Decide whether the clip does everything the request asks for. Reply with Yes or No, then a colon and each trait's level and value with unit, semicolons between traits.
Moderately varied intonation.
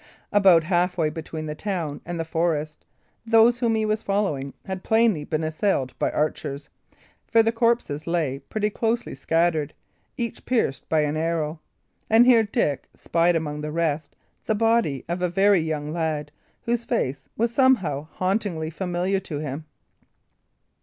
No: wide, 5.9 semitones